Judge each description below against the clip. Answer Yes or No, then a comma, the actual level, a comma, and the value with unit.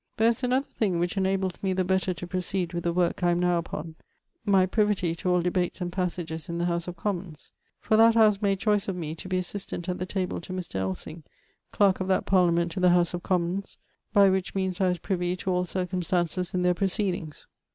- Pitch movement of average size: No, narrow, 1.8 semitones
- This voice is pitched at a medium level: Yes, medium, 180 Hz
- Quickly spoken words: Yes, fast, 230 wpm